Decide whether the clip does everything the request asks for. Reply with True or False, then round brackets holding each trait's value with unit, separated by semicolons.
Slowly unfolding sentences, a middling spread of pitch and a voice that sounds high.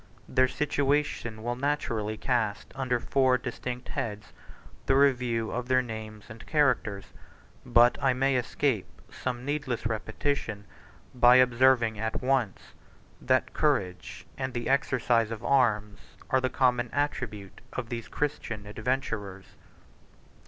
False (125 wpm; 3.1 semitones; 120 Hz)